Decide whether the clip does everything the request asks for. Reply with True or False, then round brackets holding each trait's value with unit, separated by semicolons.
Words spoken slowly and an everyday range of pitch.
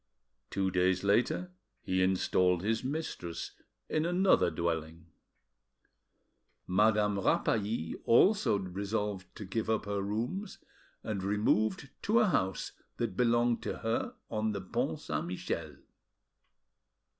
True (115 wpm; 3.8 semitones)